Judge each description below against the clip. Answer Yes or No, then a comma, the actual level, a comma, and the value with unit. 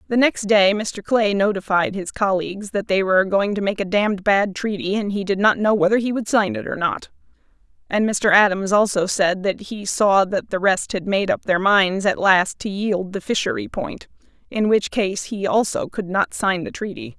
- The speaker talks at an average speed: No, fast, 220 wpm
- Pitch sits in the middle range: No, high, 200 Hz